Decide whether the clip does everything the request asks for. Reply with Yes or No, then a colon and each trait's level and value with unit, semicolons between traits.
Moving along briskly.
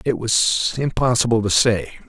No: average, 145 wpm